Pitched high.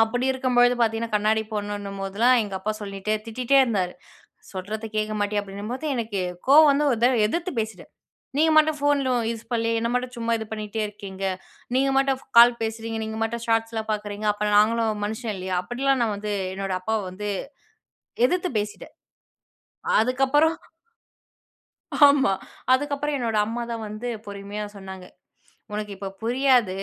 Yes: high, 225 Hz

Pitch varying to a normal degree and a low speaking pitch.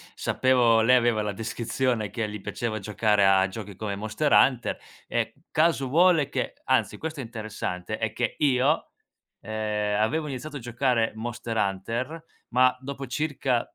Yes: average, 3.5 semitones; low, 120 Hz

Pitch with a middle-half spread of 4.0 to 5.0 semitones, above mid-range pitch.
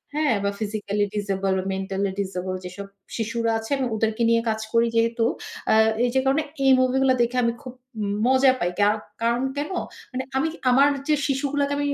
Yes: average, 4.6 semitones; high, 230 Hz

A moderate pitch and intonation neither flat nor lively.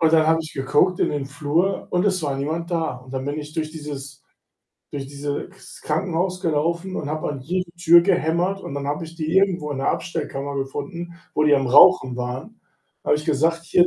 Yes: medium, 155 Hz; average, 3.3 semitones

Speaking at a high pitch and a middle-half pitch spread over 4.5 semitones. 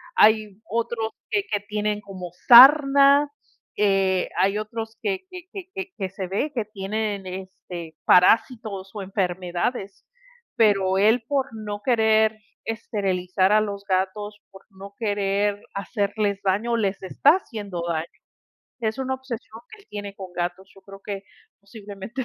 No: high, 205 Hz; average, 2.7 semitones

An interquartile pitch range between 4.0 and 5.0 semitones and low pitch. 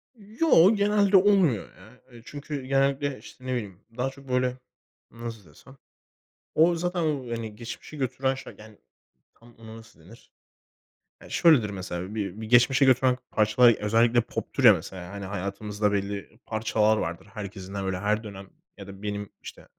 Yes: average, 4.7 semitones; low, 115 Hz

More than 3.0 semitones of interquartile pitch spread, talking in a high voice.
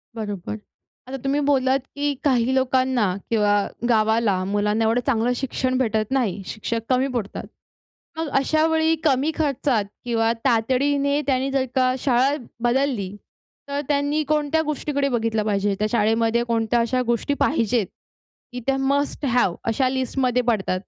Yes: average, 3.7 semitones; very high, 255 Hz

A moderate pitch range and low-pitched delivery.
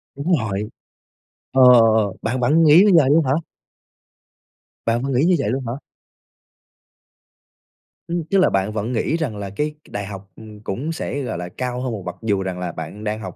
No: wide, 5.8 semitones; low, 115 Hz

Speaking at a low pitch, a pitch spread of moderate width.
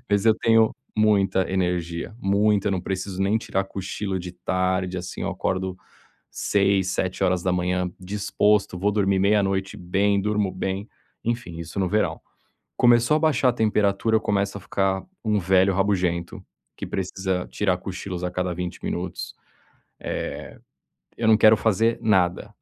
No: very low, 95 Hz; narrow, 2.2 semitones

